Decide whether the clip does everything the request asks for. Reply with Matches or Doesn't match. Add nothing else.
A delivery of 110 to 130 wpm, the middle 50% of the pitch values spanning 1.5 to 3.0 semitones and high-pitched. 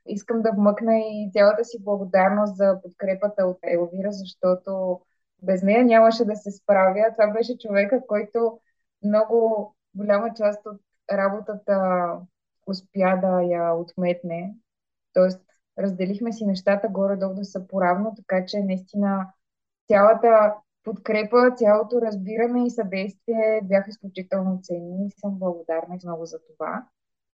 Matches